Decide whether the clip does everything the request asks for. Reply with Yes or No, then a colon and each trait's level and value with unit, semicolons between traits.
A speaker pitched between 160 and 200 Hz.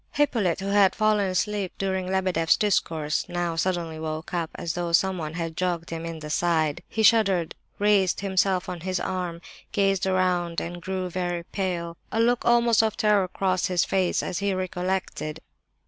Yes: medium, 185 Hz